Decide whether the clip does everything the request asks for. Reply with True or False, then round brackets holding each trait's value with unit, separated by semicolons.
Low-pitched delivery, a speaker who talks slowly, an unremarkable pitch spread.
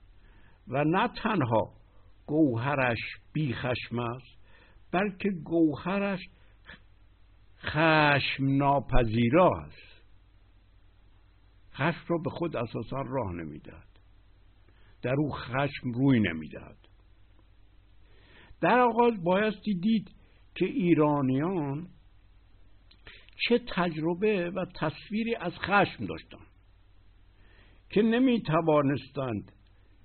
False (120 Hz; 80 wpm; 9.0 semitones)